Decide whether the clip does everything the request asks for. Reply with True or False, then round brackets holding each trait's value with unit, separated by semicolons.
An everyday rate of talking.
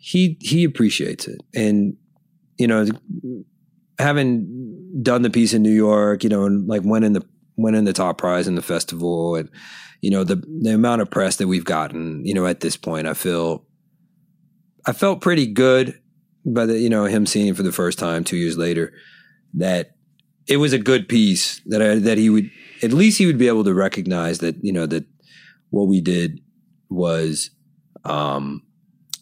True (190 wpm)